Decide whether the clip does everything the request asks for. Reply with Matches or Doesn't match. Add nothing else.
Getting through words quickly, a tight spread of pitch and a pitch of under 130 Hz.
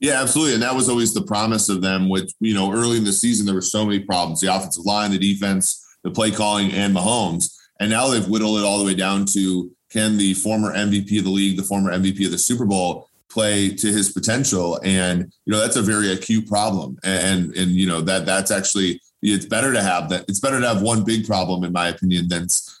Matches